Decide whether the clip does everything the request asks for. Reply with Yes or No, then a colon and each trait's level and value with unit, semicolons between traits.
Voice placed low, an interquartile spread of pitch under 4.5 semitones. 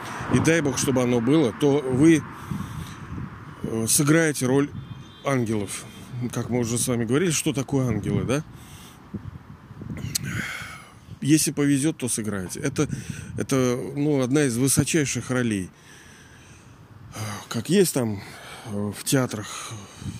Yes: low, 130 Hz; average, 3.5 semitones